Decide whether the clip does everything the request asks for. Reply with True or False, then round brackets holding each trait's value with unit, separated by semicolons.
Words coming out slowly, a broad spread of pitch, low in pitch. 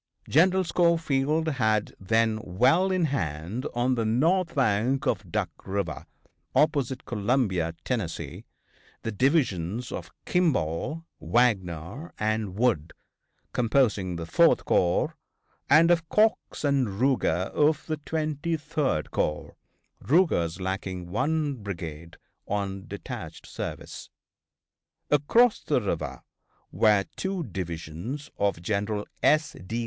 True (110 wpm; 8.2 semitones; 115 Hz)